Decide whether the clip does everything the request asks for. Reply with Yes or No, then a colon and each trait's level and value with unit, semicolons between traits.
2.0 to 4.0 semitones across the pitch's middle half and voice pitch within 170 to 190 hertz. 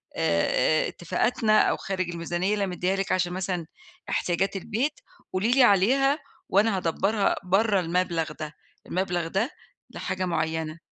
Yes: average, 3.3 semitones; medium, 185 Hz